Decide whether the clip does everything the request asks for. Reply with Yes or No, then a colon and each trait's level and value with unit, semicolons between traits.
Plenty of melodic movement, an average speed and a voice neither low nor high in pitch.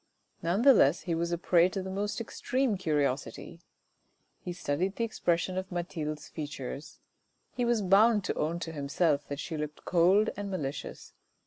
No: average, 4.6 semitones; average, 165 wpm; medium, 175 Hz